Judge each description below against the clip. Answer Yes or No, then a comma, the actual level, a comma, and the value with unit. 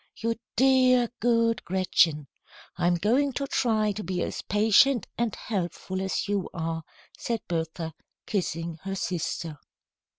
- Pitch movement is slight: No, average, 5.1 semitones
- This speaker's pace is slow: Yes, slow, 130 wpm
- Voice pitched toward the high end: Yes, high, 195 Hz